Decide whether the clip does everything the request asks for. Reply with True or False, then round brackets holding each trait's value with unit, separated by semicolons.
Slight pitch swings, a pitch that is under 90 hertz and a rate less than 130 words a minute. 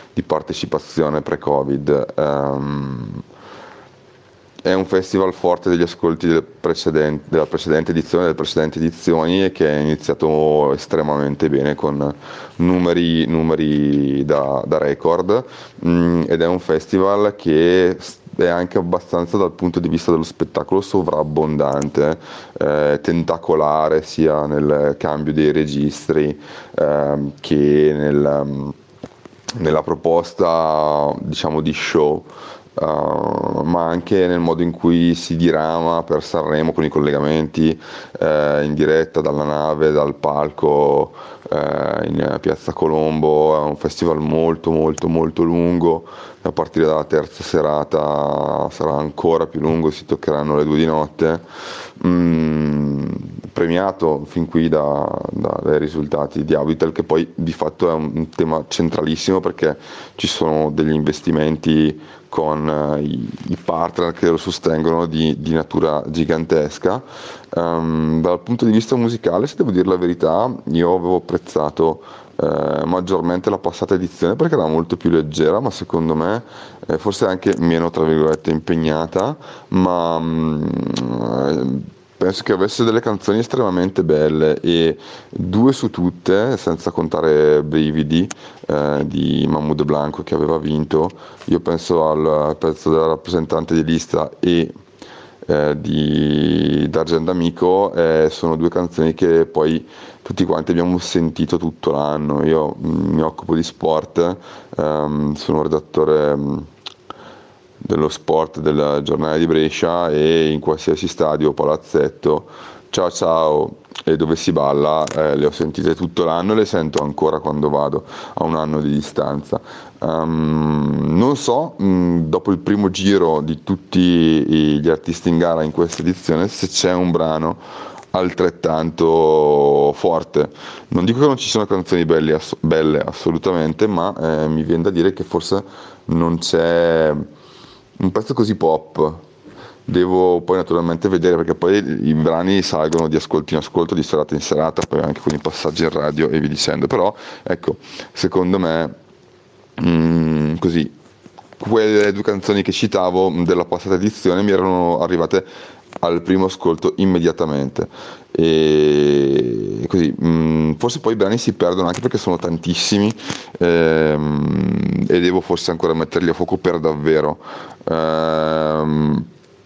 False (2.2 semitones; 80 Hz; 135 wpm)